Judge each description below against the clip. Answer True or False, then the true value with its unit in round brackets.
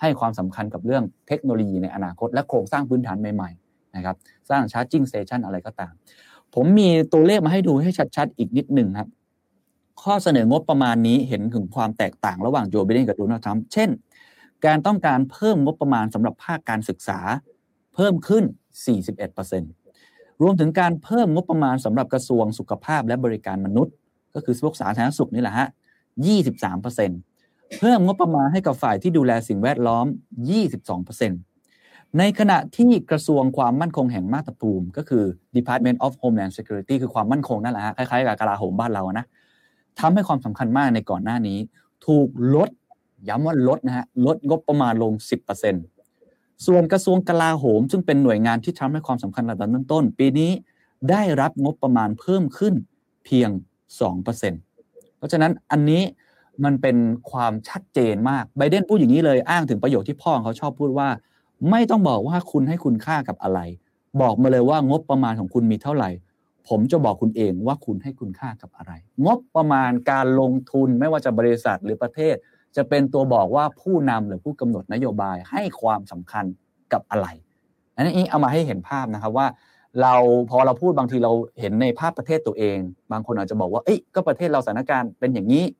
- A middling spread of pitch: False (6.0 semitones)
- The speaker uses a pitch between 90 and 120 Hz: False (130 Hz)